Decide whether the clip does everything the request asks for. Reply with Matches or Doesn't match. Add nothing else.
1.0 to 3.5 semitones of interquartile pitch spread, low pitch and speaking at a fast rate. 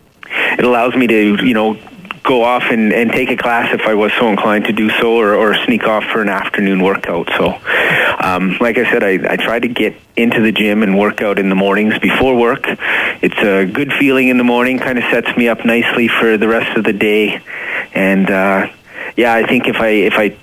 Matches